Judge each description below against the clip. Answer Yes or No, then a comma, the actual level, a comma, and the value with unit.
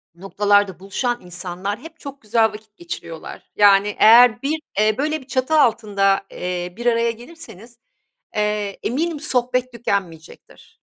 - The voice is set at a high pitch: Yes, high, 215 Hz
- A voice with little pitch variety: No, average, 4.0 semitones